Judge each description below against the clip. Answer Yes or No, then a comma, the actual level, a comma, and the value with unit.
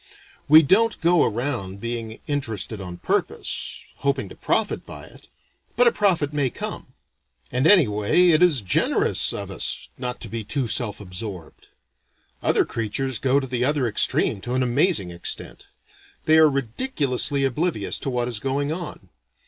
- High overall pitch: No, low, 130 Hz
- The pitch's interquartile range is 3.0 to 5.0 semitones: No, wide, 5.4 semitones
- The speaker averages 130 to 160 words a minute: Yes, average, 155 wpm